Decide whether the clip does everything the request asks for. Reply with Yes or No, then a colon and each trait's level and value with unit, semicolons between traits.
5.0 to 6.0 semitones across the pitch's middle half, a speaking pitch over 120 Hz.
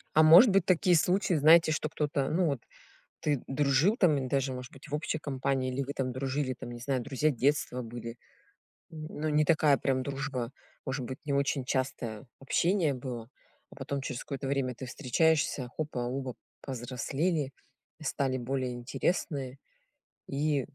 No: average, 2.9 semitones; medium, 140 Hz